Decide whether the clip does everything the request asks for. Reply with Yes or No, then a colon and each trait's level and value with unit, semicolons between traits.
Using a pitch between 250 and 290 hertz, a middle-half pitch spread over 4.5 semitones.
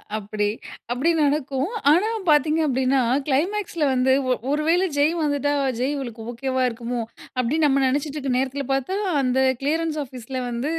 No: very high, 275 Hz; average, 3.1 semitones